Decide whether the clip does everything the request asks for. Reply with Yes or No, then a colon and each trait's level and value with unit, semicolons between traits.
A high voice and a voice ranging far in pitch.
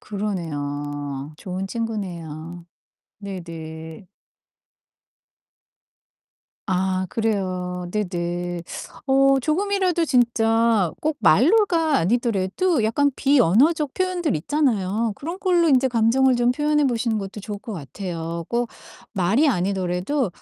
Yes: high, 215 Hz; wide, 7.3 semitones